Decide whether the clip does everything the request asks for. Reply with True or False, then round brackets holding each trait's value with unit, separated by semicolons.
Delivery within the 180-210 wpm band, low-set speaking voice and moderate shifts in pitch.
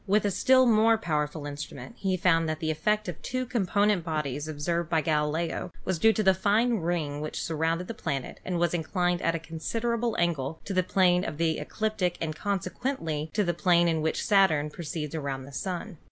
False (200 wpm; 170 Hz; 4.3 semitones)